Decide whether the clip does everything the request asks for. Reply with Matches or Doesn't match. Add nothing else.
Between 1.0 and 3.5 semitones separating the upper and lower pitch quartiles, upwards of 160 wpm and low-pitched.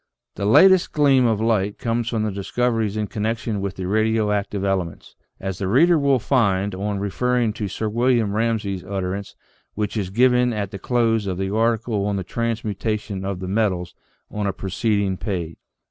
Matches